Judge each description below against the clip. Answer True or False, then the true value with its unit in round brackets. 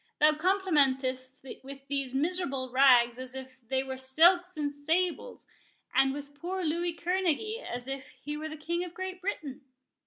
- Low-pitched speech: False (290 Hz)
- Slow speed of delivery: False (160 wpm)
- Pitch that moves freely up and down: False (4.9 semitones)